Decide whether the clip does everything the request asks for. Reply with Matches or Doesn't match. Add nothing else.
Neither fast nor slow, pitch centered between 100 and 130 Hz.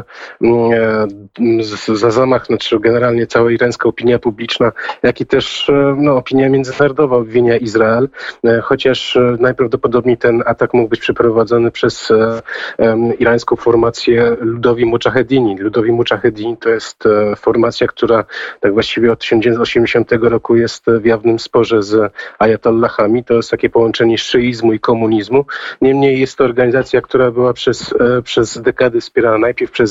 Matches